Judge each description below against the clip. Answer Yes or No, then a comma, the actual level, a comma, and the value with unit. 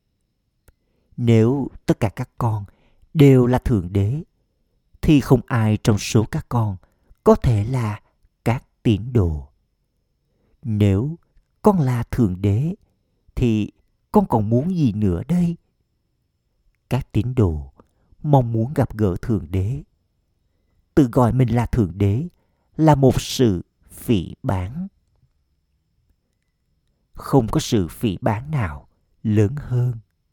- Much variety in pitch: No, average, 4.8 semitones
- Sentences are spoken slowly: Yes, slow, 125 wpm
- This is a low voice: Yes, low, 110 Hz